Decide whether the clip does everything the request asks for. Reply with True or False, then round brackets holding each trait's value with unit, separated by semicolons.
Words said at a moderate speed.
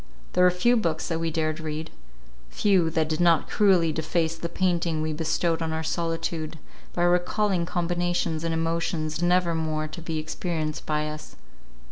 True (165 wpm)